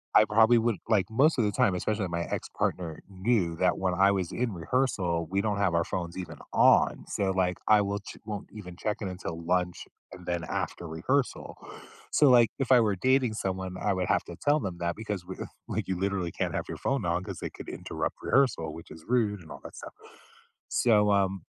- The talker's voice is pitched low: Yes, very low, 95 Hz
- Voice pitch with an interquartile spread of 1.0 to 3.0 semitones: No, average, 3.6 semitones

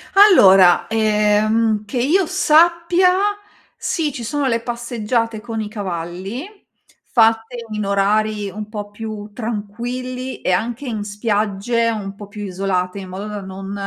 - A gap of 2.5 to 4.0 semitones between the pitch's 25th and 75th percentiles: Yes, average, 2.9 semitones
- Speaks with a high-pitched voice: Yes, high, 215 Hz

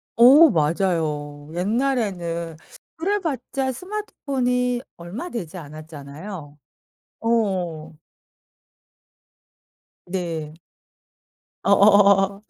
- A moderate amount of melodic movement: No, wide, 7.4 semitones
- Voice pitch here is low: No, high, 195 Hz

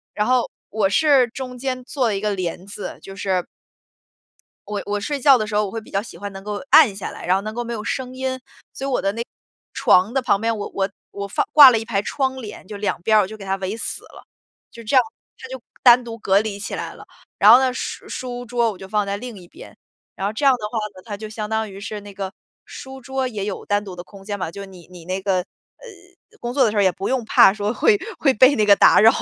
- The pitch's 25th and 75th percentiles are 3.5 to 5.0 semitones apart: Yes, average, 4.0 semitones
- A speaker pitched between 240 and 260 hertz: No, high, 215 Hz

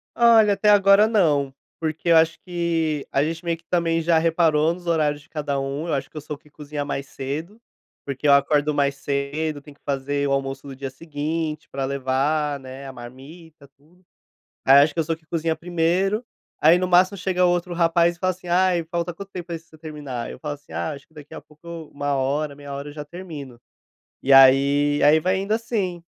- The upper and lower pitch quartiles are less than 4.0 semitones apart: Yes, average, 3.3 semitones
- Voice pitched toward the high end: No, medium, 155 Hz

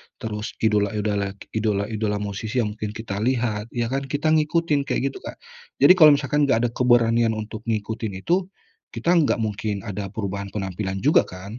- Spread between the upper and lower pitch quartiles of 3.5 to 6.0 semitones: Yes, average, 4.1 semitones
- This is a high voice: No, low, 110 Hz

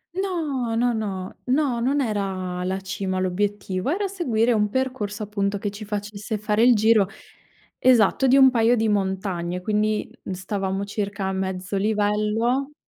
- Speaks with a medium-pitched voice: No, high, 210 Hz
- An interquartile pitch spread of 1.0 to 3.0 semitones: No, average, 3.7 semitones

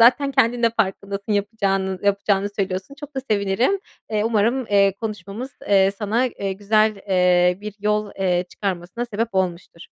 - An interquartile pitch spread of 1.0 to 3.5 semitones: Yes, average, 2.8 semitones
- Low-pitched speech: No, high, 205 Hz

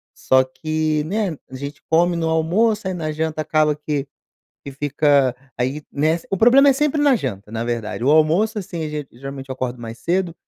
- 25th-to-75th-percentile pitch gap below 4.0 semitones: No, average, 4.5 semitones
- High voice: No, medium, 155 Hz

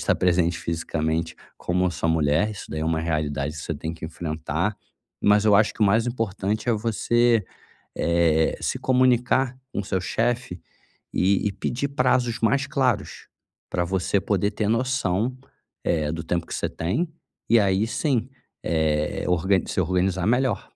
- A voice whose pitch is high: No, very low, 95 Hz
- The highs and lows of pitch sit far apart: Yes, wide, 6.0 semitones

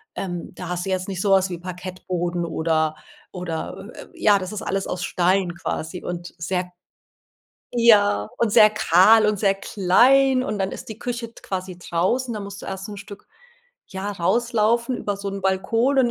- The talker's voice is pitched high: Yes, high, 195 Hz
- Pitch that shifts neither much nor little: Yes, average, 3.1 semitones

